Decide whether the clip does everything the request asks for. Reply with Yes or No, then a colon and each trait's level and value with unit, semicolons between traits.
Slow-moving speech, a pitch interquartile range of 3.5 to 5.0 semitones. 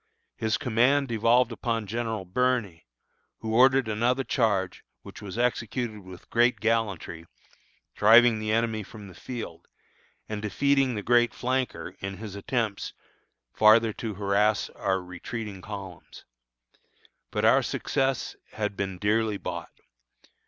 No: slow, 125 wpm; average, 3.0 semitones